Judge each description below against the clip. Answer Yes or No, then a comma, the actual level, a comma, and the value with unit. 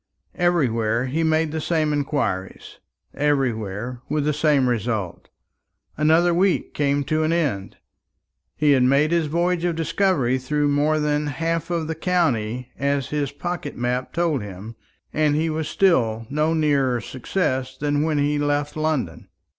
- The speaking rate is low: No, average, 145 wpm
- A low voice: No, medium, 145 Hz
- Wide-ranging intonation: No, average, 3.9 semitones